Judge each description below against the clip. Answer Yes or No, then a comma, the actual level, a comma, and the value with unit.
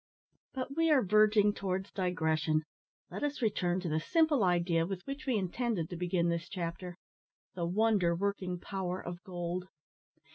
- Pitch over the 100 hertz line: Yes, medium, 185 Hz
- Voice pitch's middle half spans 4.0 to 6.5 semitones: No, average, 3.6 semitones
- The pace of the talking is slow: No, average, 155 wpm